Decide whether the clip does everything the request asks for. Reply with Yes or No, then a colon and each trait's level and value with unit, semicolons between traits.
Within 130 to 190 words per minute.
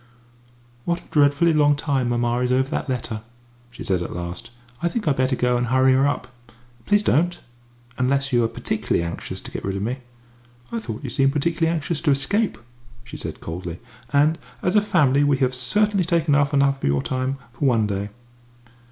No: average, 200 wpm